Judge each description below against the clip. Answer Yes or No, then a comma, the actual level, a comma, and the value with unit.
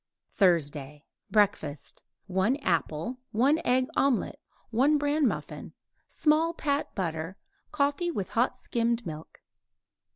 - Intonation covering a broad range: Yes, wide, 8.8 semitones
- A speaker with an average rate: No, slow, 105 wpm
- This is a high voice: Yes, high, 230 Hz